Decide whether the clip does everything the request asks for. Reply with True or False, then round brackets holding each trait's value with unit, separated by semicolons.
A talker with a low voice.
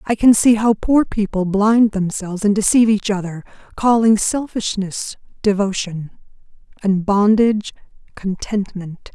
False (205 Hz)